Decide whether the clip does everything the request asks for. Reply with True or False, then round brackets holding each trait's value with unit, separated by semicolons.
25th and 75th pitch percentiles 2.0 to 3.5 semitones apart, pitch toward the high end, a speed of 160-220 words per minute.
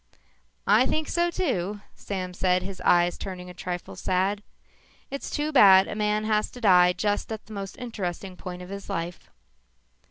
True (2.9 semitones; 195 Hz; 170 wpm)